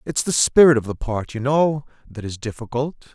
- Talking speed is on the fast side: Yes, fast, 210 wpm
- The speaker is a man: Yes, male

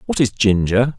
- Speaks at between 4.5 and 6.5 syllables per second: Yes, 4.7 syllables/s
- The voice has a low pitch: Yes, low, 115 Hz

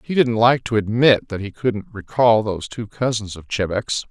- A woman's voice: No, male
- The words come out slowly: No, fast, 205 wpm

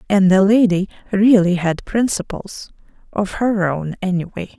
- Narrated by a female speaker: Yes, female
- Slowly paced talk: Yes, slow, 120 wpm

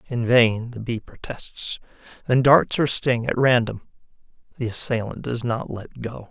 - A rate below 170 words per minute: Yes, average, 160 wpm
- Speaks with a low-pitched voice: Yes, low, 120 Hz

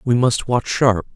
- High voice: No, low, 120 Hz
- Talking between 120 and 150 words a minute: No, fast, 205 wpm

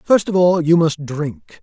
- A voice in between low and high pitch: Yes, medium, 160 Hz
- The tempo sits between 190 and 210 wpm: No, fast, 220 wpm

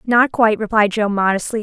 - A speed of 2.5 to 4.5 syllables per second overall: No, 5.8 syllables/s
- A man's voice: No, female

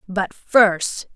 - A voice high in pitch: Yes, high, 195 Hz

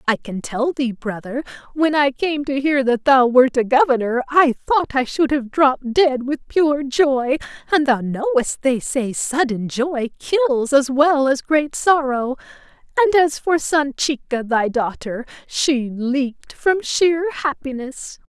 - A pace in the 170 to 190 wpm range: No, average, 160 wpm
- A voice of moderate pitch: No, very high, 275 Hz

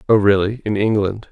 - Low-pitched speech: Yes, low, 105 Hz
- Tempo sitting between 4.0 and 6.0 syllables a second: Yes, 5.5 syllables/s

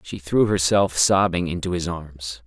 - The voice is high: No, very low, 85 Hz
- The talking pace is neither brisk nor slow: Yes, average, 170 wpm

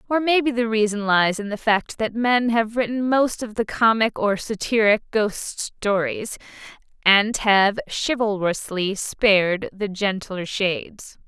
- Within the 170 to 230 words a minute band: No, average, 145 wpm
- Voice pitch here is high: Yes, high, 215 Hz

